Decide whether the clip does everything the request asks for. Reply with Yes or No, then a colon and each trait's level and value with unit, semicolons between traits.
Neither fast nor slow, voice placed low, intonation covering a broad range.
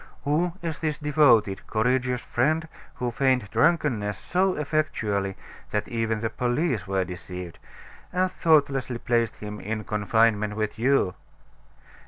No: slow, 125 wpm; low, 120 Hz; wide, 6.1 semitones